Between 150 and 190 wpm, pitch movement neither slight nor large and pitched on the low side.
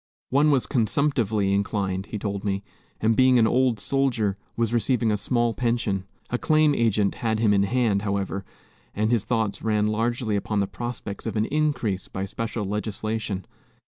Yes: average, 170 wpm; average, 3.2 semitones; low, 110 Hz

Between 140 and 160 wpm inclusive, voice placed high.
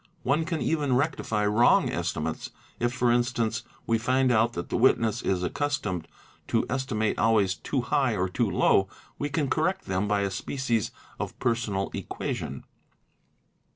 No: average, 155 wpm; low, 120 Hz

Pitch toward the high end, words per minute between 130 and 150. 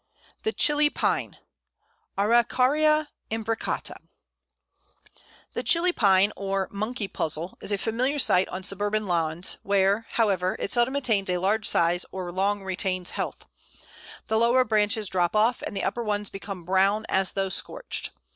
Yes: high, 205 Hz; average, 145 wpm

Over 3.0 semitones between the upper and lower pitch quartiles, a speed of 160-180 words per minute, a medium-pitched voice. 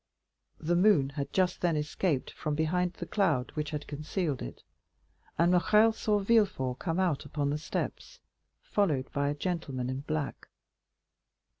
No: average, 4.3 semitones; average, 150 wpm; medium, 155 Hz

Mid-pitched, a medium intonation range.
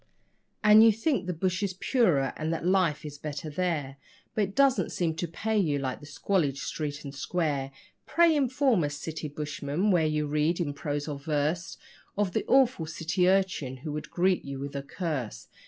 Yes: medium, 160 Hz; average, 4.6 semitones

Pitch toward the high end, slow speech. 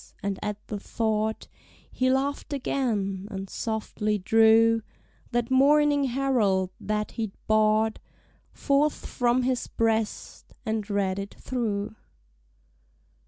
Yes: high, 220 Hz; slow, 110 wpm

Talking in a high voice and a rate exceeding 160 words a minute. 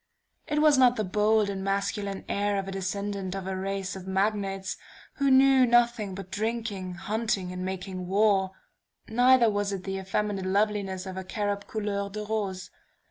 Yes: high, 200 Hz; average, 170 wpm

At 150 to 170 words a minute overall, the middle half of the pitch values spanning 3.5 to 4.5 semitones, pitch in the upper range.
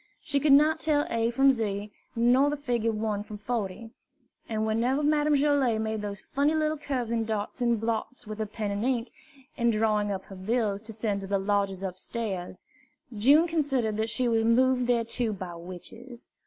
No: average, 180 wpm; average, 3.8 semitones; high, 230 Hz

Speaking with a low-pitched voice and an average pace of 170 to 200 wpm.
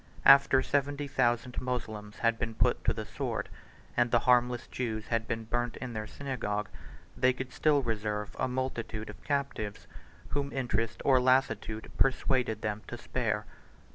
No: low, 120 Hz; average, 155 wpm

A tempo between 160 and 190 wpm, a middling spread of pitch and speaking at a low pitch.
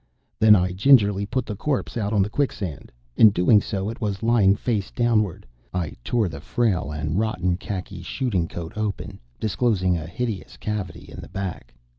Yes: average, 175 wpm; average, 3.5 semitones; low, 100 Hz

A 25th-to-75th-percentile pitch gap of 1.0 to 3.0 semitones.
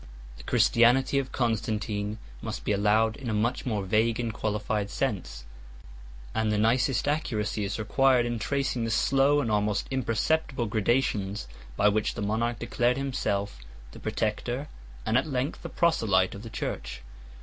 No: average, 3.4 semitones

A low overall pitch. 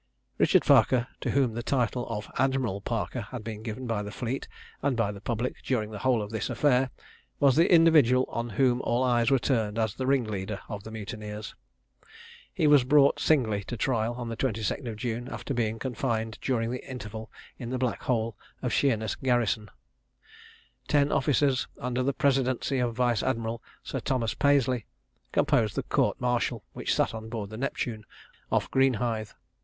Yes: low, 120 Hz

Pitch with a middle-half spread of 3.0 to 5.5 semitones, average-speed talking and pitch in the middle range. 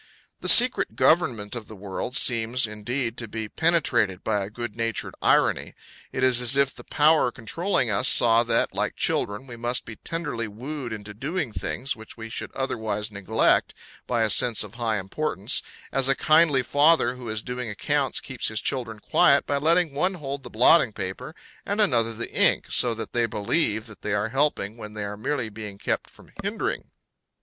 No: average, 4.4 semitones; average, 190 wpm; low, 120 Hz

